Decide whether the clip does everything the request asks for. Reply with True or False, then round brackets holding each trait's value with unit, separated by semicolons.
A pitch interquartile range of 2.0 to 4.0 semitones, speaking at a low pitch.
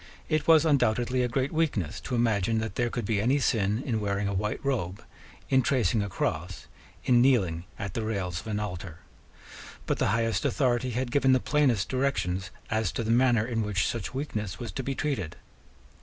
False (4.4 semitones; 115 Hz)